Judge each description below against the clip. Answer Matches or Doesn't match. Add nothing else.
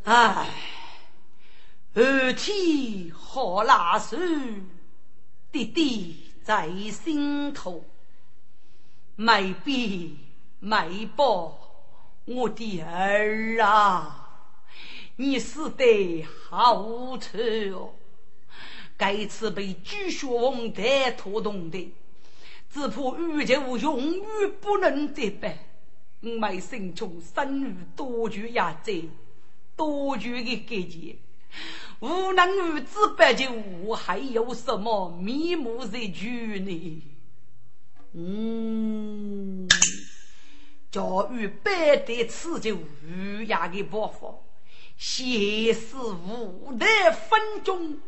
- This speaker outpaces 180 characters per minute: Doesn't match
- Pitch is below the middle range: Doesn't match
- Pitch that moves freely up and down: Matches